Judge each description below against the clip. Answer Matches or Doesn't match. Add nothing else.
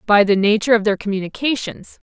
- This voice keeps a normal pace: Matches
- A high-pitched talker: Matches